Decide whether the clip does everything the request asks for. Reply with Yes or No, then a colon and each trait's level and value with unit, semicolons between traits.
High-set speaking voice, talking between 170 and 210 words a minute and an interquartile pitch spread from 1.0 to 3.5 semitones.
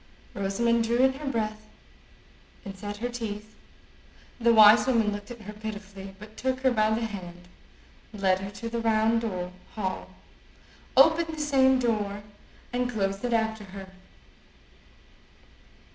No: high, 220 Hz; average, 140 wpm; average, 2.8 semitones